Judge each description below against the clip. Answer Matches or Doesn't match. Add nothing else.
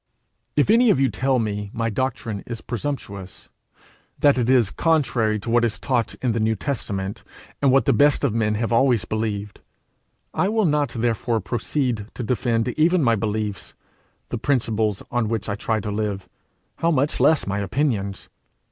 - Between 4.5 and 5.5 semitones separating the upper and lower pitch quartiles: Doesn't match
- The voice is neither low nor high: Doesn't match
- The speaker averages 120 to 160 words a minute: Doesn't match